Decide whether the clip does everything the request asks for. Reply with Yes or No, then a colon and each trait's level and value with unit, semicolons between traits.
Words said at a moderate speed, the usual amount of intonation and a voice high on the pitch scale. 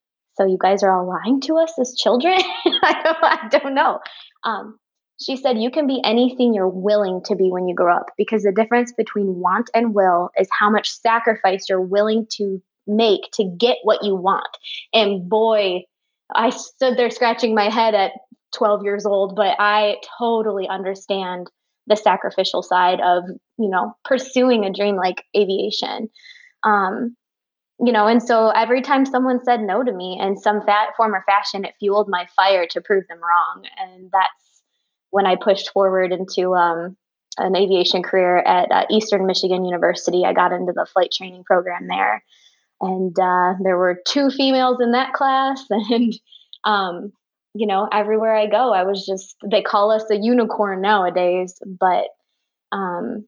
Yes: average, 175 wpm; average, 3.8 semitones; high, 205 Hz